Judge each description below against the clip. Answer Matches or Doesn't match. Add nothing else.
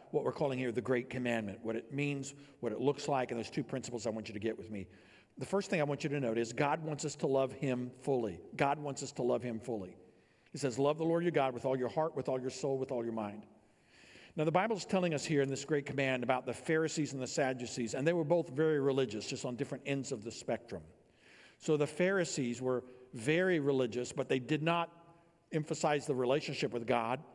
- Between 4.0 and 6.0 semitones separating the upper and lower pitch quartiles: Doesn't match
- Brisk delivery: Matches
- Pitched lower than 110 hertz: Doesn't match